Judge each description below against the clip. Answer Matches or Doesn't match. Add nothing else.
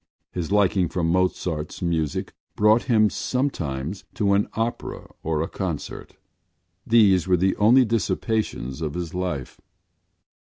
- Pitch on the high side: Doesn't match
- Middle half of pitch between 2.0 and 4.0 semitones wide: Doesn't match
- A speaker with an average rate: Doesn't match